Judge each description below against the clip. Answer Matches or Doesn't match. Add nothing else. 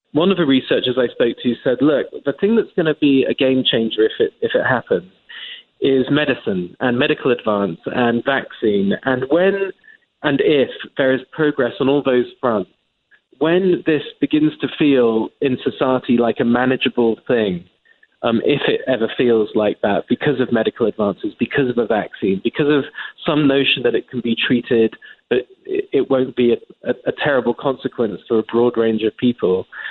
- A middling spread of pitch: Doesn't match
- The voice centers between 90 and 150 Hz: Matches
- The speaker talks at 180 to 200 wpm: Matches